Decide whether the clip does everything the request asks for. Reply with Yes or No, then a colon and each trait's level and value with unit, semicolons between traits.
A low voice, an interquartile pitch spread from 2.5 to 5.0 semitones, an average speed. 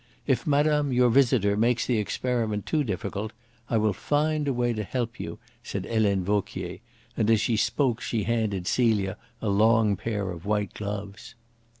Yes: low, 110 Hz; average, 3.1 semitones; average, 170 wpm